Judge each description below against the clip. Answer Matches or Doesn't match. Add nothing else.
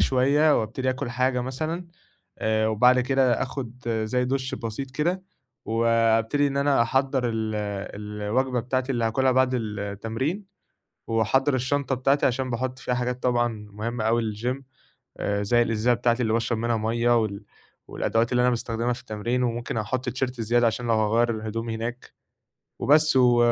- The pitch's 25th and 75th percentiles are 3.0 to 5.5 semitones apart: Doesn't match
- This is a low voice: Matches